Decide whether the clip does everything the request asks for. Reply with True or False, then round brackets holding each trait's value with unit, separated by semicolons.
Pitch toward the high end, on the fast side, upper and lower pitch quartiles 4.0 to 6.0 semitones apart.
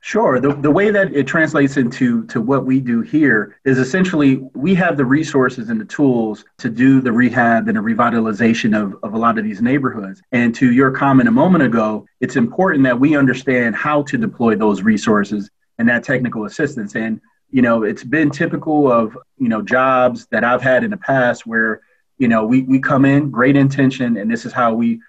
False (130 Hz; 210 wpm; 4.6 semitones)